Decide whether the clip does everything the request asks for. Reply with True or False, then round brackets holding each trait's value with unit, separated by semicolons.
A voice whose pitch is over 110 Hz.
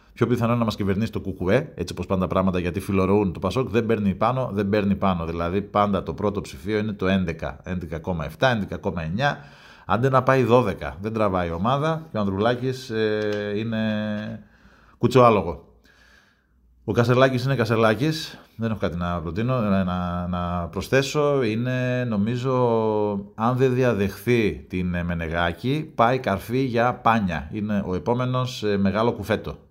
False (105 Hz)